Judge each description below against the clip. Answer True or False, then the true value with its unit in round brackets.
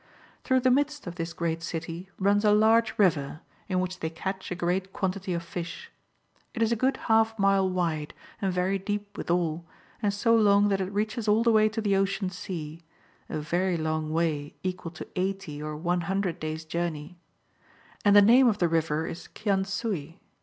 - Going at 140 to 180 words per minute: False (190 wpm)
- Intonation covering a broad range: False (3.6 semitones)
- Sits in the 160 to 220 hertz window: True (185 Hz)